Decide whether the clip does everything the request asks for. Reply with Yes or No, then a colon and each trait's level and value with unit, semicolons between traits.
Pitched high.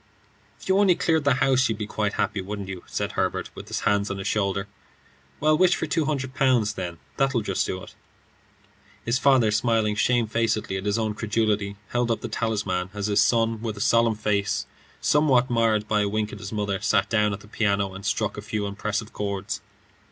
No: low, 105 Hz